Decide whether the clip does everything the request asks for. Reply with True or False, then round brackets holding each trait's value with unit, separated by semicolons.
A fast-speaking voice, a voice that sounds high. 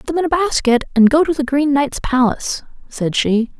True (235 wpm; 275 Hz)